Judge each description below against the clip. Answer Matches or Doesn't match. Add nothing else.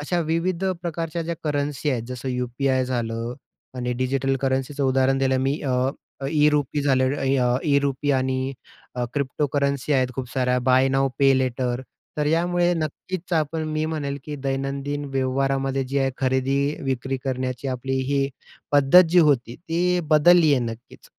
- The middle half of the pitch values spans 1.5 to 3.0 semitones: Matches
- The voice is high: Doesn't match